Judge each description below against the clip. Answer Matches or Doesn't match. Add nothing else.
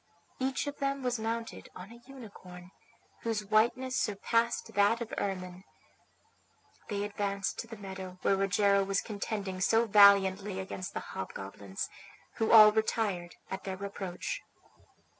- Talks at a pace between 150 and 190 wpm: Doesn't match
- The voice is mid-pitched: Doesn't match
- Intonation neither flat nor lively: Matches